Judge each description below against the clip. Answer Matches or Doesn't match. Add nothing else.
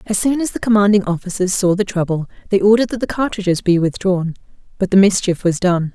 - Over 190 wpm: Matches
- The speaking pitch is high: Matches